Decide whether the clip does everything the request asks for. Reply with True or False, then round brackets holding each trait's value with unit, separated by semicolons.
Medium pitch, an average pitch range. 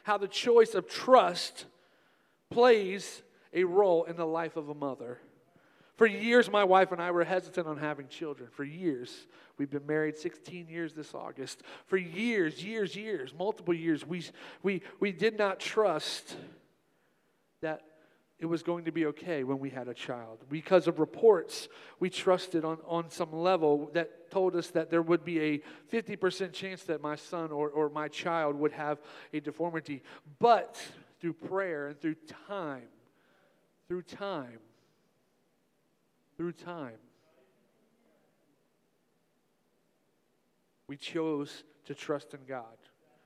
True (170 Hz; 4.1 semitones)